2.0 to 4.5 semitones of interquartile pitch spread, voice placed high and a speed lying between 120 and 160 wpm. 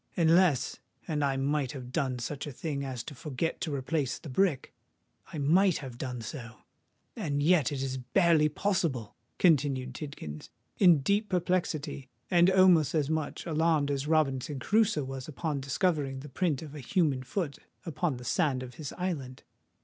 No: average, 3.9 semitones; medium, 145 Hz; average, 155 wpm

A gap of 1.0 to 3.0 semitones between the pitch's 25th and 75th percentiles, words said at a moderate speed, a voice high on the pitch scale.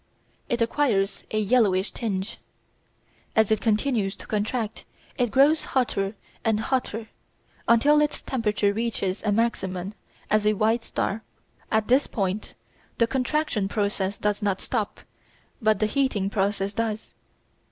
No: average, 2.7 semitones; slow, 130 wpm; high, 215 Hz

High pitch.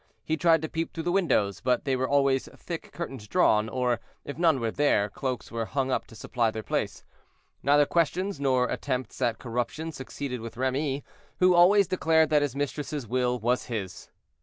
No: low, 135 Hz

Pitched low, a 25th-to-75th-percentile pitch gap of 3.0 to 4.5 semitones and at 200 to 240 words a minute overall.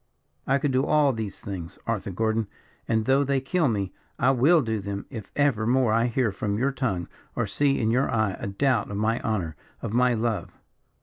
Yes: low, 115 Hz; average, 4.2 semitones; fast, 205 wpm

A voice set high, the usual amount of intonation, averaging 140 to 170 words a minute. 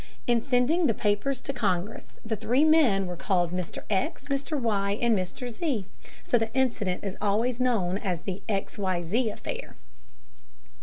Yes: high, 220 Hz; average, 4.6 semitones; average, 155 wpm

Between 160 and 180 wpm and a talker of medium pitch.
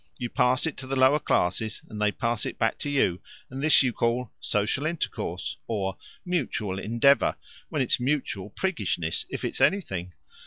No: average, 170 wpm; low, 120 Hz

